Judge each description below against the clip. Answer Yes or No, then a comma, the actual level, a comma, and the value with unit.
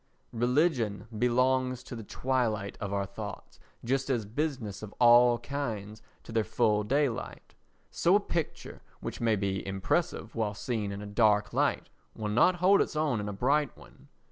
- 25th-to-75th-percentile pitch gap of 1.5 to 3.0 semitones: No, average, 4.1 semitones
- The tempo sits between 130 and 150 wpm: No, average, 170 wpm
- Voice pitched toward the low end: Yes, low, 115 Hz